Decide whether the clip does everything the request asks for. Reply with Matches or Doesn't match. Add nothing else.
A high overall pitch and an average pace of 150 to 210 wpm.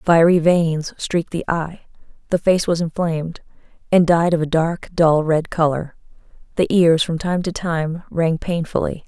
Doesn't match